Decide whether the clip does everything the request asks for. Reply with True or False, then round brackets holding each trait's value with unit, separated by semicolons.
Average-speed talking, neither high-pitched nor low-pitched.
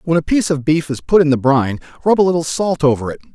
False (285 wpm; 155 Hz)